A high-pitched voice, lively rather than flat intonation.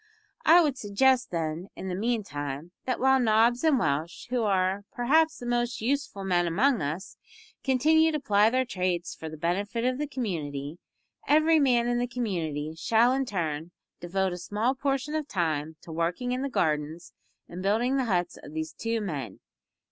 Yes: high, 210 Hz; wide, 7.1 semitones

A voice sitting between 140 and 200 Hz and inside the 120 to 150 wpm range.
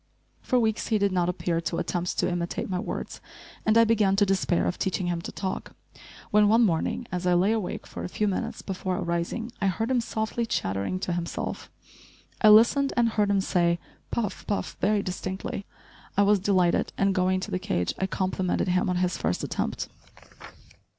No: high, 190 Hz; average, 190 wpm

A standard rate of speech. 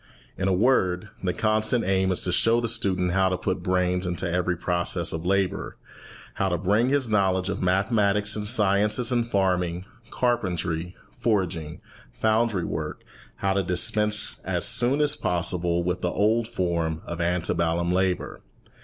Yes: average, 160 wpm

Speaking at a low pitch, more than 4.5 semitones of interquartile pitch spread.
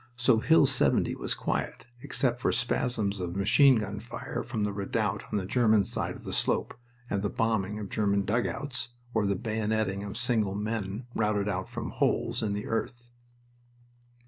No: low, 110 Hz; average, 2.8 semitones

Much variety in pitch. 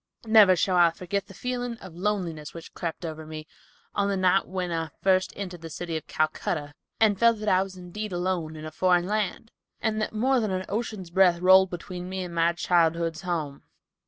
No: average, 3.1 semitones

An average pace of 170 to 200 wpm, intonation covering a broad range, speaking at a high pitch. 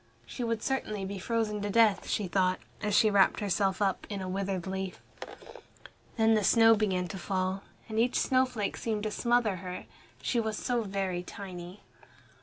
No: average, 175 wpm; average, 2.8 semitones; high, 205 Hz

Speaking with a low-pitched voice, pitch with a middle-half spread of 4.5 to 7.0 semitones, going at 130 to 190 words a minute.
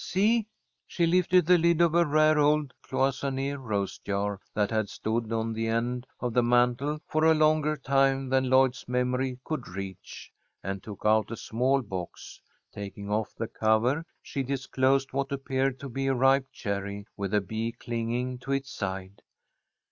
No: low, 125 Hz; average, 4.0 semitones; average, 170 wpm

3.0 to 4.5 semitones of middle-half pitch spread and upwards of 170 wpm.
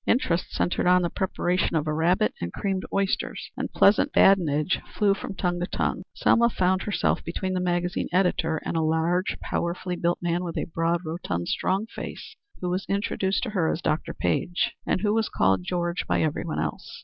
No: narrow, 2.5 semitones; average, 195 wpm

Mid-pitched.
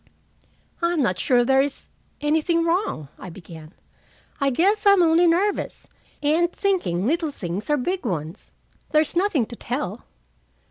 No: very high, 295 Hz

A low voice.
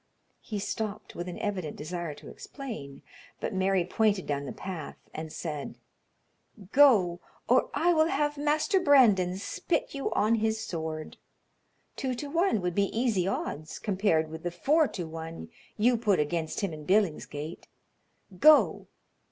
No: high, 195 Hz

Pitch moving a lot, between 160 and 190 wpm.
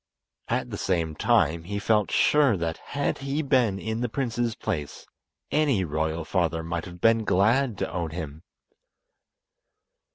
No: wide, 6.4 semitones; average, 150 wpm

